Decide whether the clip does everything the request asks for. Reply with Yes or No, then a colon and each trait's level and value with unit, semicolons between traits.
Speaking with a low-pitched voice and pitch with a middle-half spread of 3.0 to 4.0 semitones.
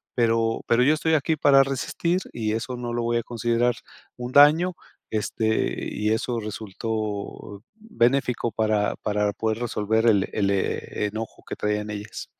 No: low, 115 Hz; narrow, 2.6 semitones